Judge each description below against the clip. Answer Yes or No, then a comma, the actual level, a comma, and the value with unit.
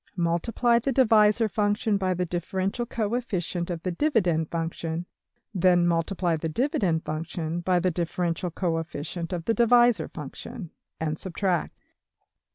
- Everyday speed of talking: No, slow, 130 wpm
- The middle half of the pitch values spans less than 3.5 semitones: No, average, 4.1 semitones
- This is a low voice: No, medium, 180 Hz